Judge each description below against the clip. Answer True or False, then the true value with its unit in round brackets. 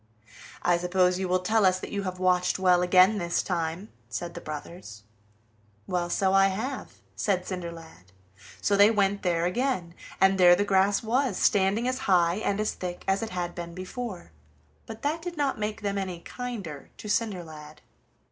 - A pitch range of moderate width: True (3.0 semitones)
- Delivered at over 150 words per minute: True (175 wpm)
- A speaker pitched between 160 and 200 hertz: True (185 Hz)